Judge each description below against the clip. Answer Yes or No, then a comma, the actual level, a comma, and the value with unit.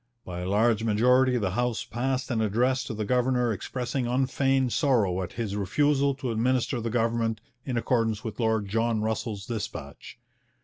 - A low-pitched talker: Yes, low, 115 Hz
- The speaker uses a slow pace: No, average, 165 wpm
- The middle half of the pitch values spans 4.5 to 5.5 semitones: No, average, 2.7 semitones